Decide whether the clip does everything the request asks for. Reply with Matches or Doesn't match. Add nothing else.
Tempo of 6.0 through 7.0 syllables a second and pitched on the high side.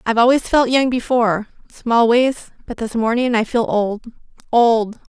Doesn't match